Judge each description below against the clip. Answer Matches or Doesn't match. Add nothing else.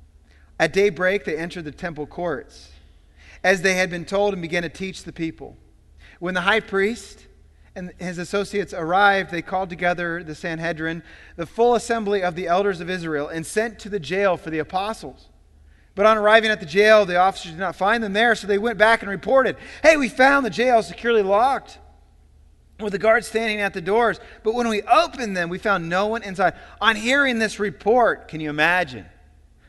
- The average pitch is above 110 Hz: Matches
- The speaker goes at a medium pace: Matches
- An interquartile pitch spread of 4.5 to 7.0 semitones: Matches